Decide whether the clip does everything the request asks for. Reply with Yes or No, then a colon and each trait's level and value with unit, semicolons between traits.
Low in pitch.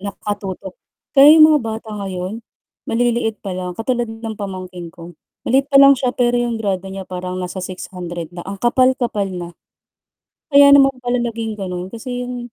No: high, 220 Hz